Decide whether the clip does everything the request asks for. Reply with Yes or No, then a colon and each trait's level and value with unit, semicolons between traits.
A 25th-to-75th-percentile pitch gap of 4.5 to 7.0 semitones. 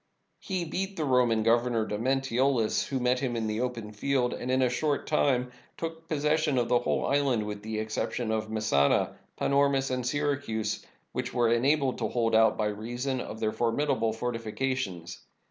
No: average, 3.8 semitones